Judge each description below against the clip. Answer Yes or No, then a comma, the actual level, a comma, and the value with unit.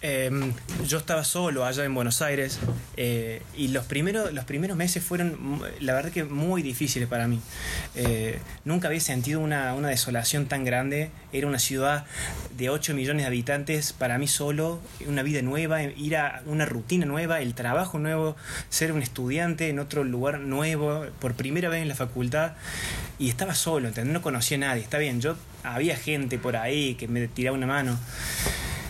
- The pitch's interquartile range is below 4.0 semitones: Yes, average, 3.6 semitones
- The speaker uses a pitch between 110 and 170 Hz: Yes, medium, 140 Hz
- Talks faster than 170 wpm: Yes, average, 180 wpm